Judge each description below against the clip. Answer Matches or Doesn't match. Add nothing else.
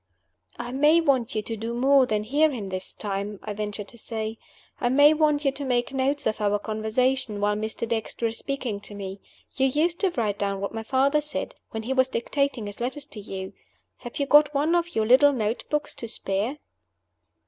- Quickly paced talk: Matches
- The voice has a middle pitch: Doesn't match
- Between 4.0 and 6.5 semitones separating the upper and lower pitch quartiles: Matches